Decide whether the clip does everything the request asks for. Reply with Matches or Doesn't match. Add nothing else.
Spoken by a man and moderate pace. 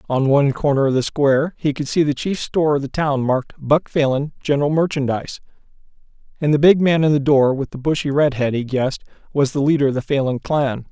Doesn't match